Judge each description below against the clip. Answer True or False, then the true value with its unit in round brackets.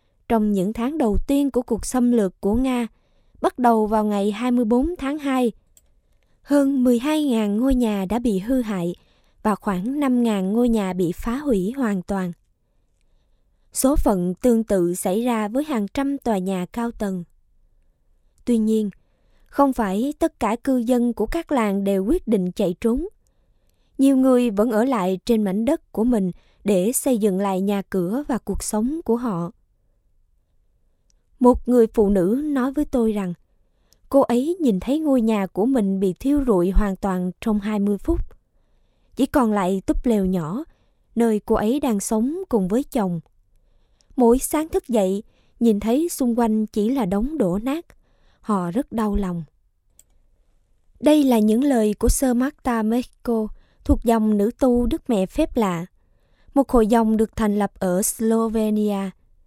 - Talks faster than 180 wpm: False (165 wpm)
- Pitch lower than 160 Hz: False (220 Hz)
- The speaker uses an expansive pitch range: False (4.7 semitones)